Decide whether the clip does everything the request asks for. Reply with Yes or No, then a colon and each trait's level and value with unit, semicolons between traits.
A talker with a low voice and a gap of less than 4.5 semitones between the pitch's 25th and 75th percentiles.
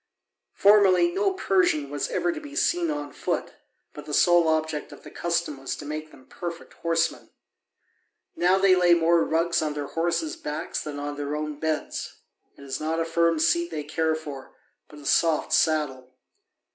No: medium, 165 Hz; average, 3.4 semitones